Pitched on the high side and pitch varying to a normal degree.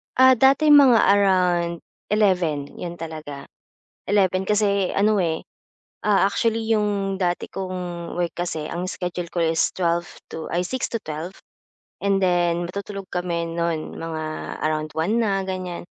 No: medium, 180 Hz; average, 3.0 semitones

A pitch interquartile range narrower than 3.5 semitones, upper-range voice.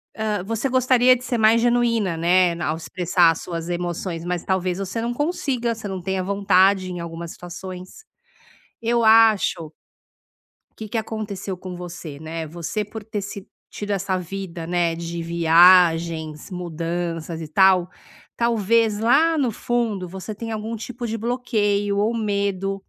No: average, 4.3 semitones; high, 195 Hz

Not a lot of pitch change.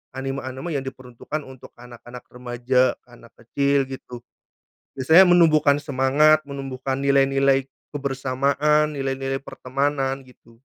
Yes: narrow, 1.7 semitones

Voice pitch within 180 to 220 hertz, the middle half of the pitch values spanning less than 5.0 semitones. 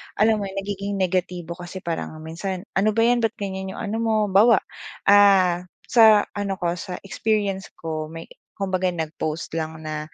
Yes: high, 190 Hz; average, 3.0 semitones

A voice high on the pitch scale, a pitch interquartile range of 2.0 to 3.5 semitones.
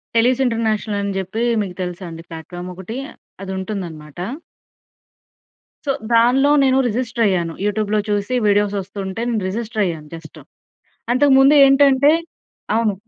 No: high, 210 Hz; average, 4.2 semitones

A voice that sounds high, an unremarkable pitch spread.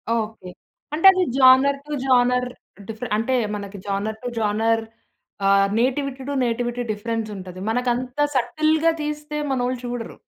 Yes: high, 245 Hz; average, 3.3 semitones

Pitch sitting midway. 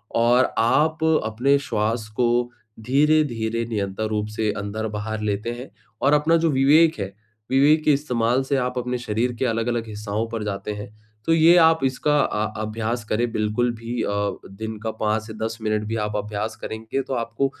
No: low, 115 Hz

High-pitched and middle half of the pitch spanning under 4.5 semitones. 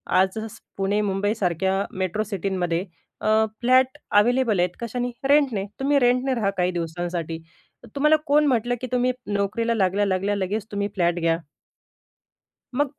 No: high, 205 Hz; average, 5.1 semitones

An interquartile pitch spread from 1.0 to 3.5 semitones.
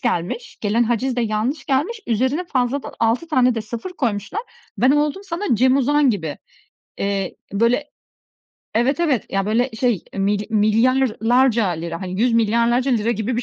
No: average, 3.9 semitones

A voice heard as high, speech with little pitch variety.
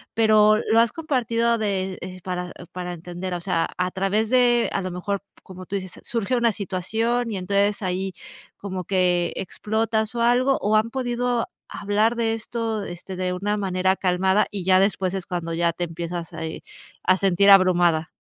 No: high, 195 Hz; average, 3.6 semitones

